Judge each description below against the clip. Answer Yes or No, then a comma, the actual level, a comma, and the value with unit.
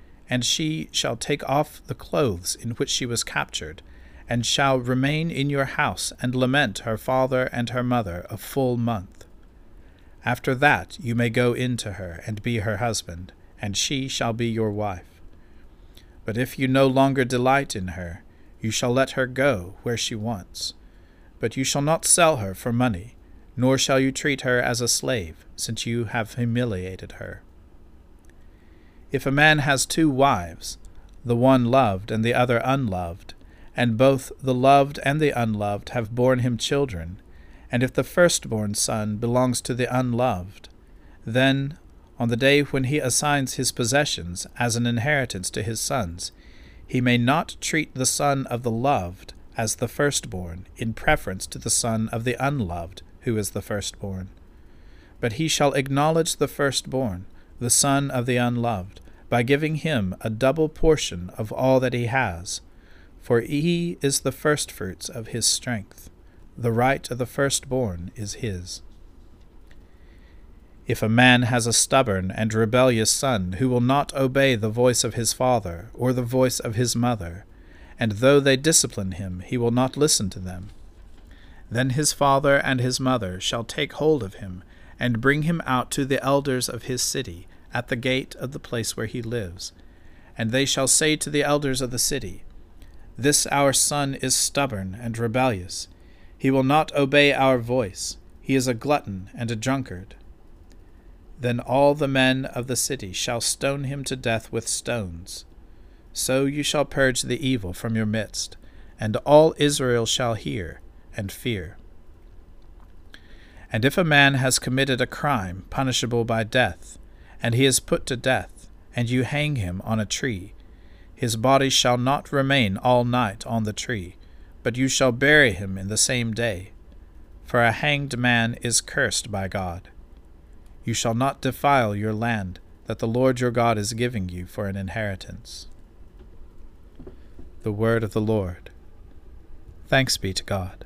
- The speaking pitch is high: No, low, 115 Hz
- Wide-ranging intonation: Yes, wide, 6.5 semitones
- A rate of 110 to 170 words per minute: Yes, average, 165 wpm